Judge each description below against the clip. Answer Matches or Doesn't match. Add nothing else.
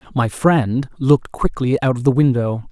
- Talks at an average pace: Matches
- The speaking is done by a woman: Doesn't match